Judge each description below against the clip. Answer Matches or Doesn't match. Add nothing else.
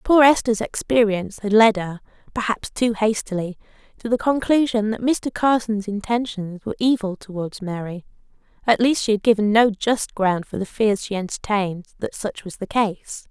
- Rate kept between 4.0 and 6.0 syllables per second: Matches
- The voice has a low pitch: Doesn't match